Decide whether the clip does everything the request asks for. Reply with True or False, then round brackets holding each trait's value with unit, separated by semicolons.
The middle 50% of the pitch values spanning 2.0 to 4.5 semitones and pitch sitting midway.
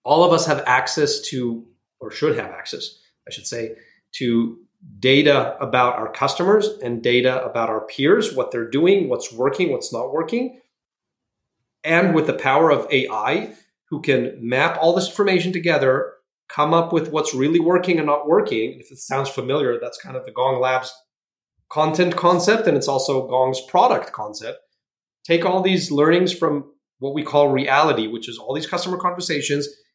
False (5.5 semitones; 145 Hz)